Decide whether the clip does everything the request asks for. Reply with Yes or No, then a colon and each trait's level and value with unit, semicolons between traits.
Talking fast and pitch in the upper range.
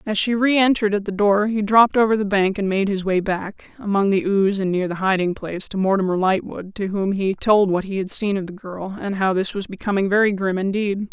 Yes: fast, 250 wpm; high, 200 Hz